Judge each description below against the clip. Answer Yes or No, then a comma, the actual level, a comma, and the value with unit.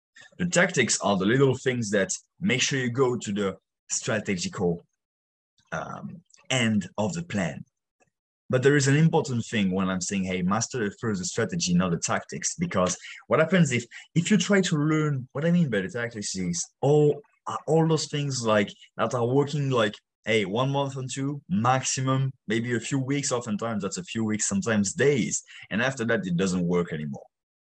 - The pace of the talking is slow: No, average, 185 wpm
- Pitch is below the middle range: Yes, low, 125 Hz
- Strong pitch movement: Yes, wide, 6.5 semitones